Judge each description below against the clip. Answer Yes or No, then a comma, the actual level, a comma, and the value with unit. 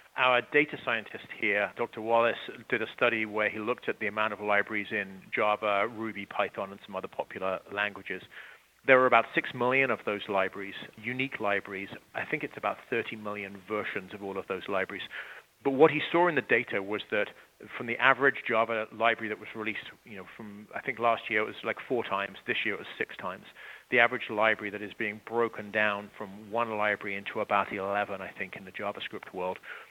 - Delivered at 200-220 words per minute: Yes, fast, 205 wpm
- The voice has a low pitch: Yes, low, 110 Hz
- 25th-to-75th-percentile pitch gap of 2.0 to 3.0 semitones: Yes, narrow, 2.4 semitones